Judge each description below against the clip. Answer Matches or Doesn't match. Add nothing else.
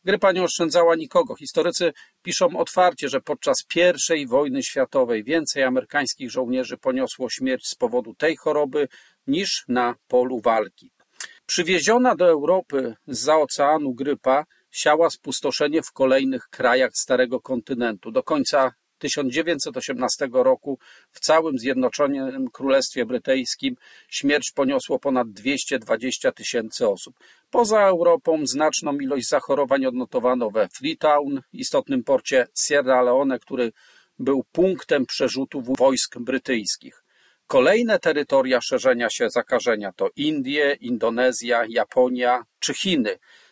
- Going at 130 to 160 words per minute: Doesn't match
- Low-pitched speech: Doesn't match